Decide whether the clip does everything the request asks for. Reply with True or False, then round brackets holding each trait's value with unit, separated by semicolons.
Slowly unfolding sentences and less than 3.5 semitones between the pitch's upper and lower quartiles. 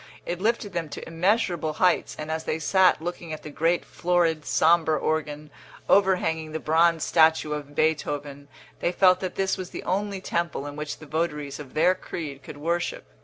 False (180 wpm; 2.8 semitones)